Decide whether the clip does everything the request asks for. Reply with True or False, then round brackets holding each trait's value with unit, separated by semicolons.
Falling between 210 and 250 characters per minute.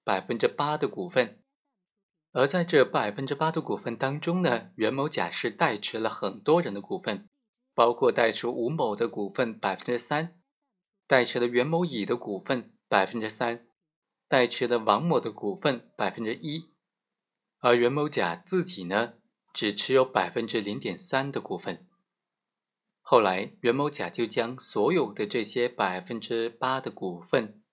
True (235 characters per minute)